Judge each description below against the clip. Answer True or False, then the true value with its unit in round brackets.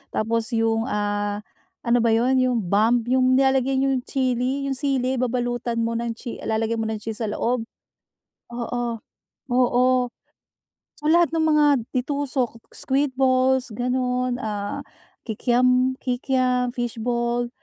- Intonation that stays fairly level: True (2.2 semitones)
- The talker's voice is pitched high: True (245 Hz)